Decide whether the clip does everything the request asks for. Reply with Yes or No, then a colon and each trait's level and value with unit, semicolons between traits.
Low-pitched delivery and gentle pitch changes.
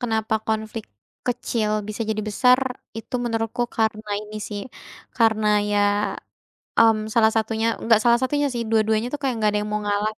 No: high, 220 Hz; narrow, 1.6 semitones